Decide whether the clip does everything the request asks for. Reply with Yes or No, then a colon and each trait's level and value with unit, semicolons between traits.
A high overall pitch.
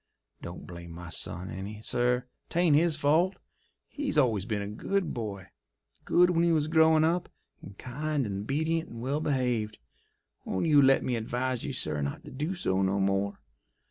No: low, 125 Hz